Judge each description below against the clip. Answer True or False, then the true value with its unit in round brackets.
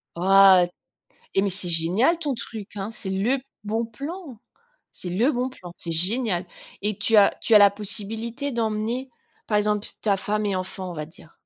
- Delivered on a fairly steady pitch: False (3.5 semitones)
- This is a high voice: True (210 Hz)